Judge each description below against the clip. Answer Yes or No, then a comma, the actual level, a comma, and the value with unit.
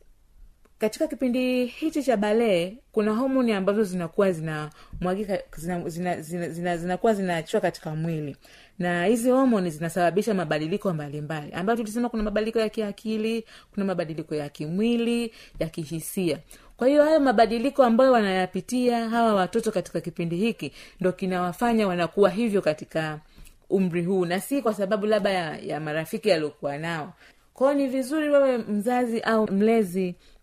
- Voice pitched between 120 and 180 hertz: No, high, 200 Hz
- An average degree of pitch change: Yes, average, 5.0 semitones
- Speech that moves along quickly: Yes, fast, 150 wpm